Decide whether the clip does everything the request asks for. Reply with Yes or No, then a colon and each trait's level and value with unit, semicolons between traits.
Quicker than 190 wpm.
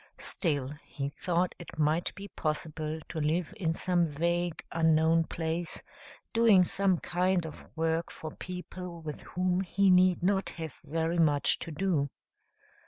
No: average, 145 wpm